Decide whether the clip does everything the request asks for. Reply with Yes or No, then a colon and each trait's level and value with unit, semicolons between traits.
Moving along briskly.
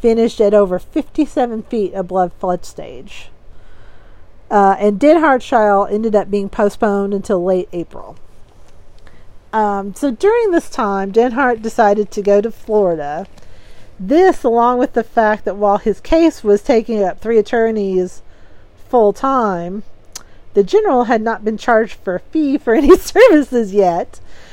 No: average, 145 wpm